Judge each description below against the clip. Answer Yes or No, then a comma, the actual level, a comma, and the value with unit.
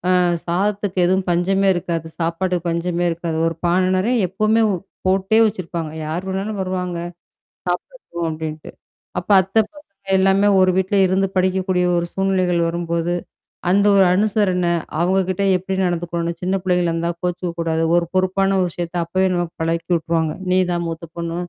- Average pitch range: No, narrow, 2.0 semitones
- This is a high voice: No, medium, 180 Hz